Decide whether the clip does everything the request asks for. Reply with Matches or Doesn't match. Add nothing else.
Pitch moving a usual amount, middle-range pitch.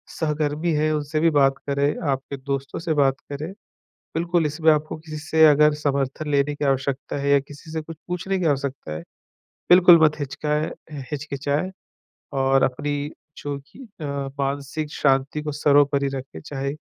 Doesn't match